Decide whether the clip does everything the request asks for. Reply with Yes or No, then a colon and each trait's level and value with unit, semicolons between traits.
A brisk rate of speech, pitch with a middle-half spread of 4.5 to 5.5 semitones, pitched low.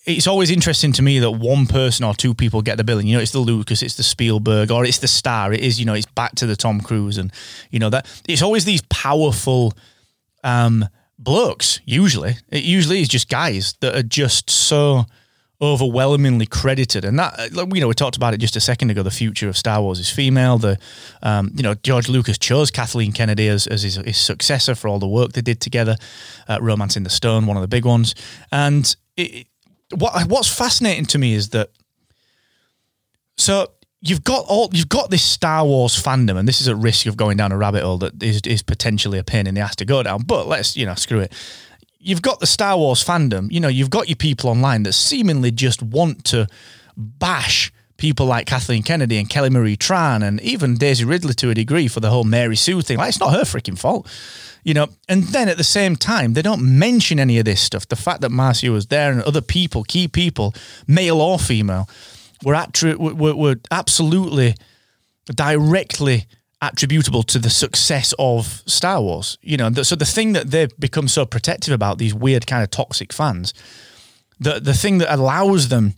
Yes: fast, 210 wpm; average, 5.1 semitones; low, 125 Hz